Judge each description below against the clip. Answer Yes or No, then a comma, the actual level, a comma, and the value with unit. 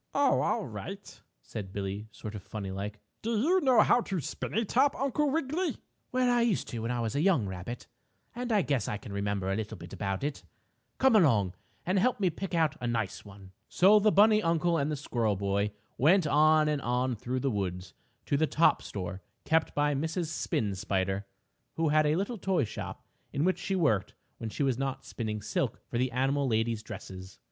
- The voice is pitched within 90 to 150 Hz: Yes, low, 135 Hz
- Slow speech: No, fast, 205 wpm